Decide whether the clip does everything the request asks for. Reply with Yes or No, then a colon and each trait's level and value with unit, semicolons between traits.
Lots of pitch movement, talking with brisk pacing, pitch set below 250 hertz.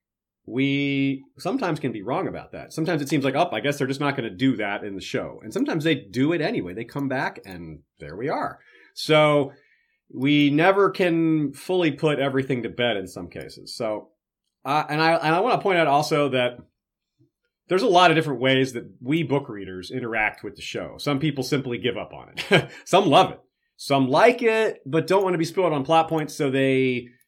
No: average, 4.6 semitones; fast, 220 wpm; medium, 140 Hz